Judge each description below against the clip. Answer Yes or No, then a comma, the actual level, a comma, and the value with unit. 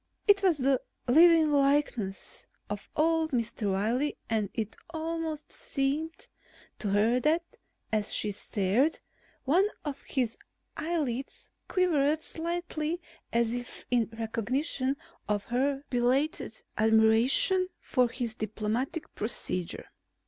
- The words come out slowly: Yes, slow, 110 wpm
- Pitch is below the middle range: No, very high, 265 Hz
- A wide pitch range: Yes, wide, 6.0 semitones